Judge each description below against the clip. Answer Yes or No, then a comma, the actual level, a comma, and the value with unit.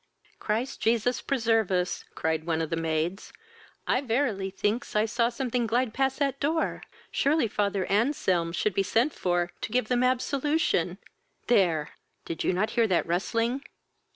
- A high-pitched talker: Yes, high, 225 Hz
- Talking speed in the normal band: Yes, average, 155 wpm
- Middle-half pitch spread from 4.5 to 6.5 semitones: Yes, wide, 5.6 semitones